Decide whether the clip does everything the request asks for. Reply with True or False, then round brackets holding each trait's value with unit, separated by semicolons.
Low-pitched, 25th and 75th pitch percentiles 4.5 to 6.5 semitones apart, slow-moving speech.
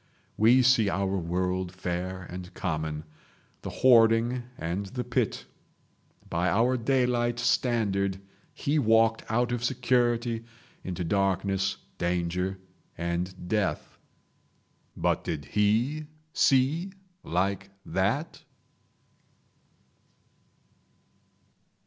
True (100 Hz; 4.9 semitones; 90 wpm)